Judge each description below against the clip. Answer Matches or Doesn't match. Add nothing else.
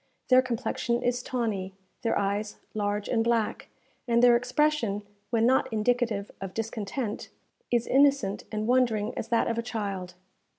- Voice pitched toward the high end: Matches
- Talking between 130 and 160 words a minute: Matches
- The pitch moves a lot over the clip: Doesn't match